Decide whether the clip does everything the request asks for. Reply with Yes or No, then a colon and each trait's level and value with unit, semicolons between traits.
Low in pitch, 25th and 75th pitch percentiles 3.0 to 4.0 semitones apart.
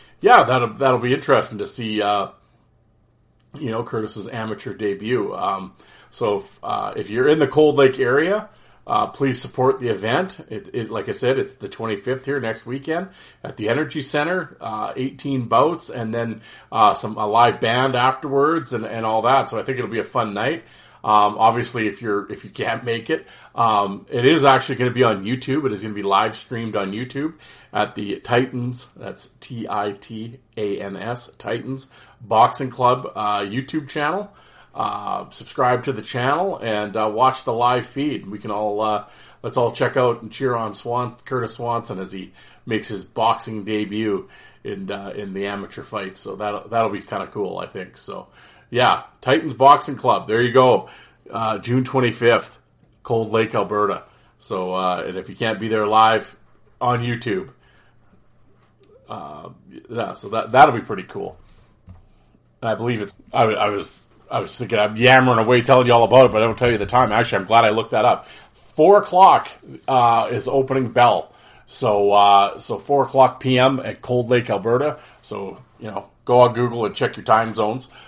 Yes: low, 120 Hz; average, 3.4 semitones